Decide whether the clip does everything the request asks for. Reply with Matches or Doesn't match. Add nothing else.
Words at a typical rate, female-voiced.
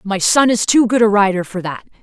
Doesn't match